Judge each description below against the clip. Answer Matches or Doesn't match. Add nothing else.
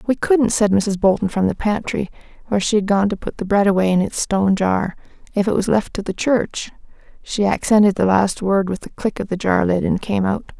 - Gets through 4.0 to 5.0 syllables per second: Doesn't match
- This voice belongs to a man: Doesn't match